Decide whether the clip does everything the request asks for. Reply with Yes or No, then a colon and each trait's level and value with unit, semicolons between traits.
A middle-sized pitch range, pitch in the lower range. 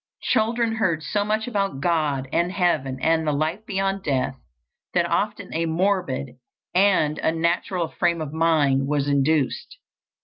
No: average, 5.0 semitones; medium, 165 Hz